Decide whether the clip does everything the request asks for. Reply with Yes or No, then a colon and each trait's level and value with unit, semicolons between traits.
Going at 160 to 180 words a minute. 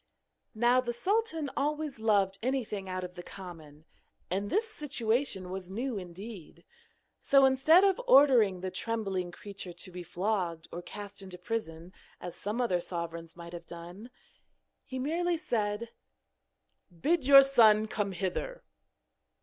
No: average, 140 wpm